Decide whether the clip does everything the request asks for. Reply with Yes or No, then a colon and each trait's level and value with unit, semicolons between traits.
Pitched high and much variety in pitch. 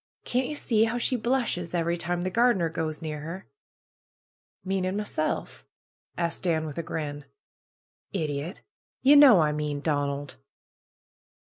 No: medium, 170 Hz; wide, 5.7 semitones